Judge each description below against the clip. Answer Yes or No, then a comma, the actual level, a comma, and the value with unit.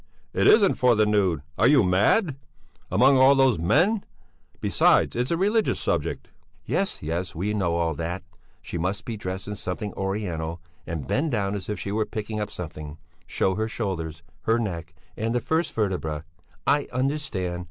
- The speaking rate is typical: Yes, average, 175 wpm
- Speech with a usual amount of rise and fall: No, wide, 6.5 semitones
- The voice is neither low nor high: No, low, 105 Hz